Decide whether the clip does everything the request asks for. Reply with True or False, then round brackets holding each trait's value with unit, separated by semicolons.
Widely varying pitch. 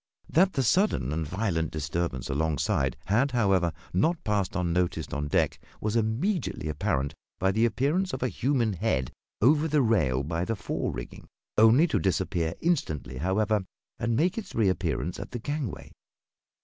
True (7.8 semitones)